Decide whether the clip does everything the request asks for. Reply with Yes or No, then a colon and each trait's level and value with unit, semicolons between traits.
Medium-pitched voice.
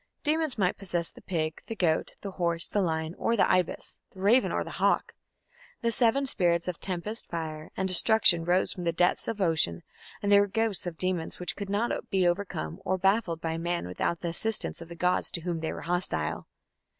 Yes: medium, 180 Hz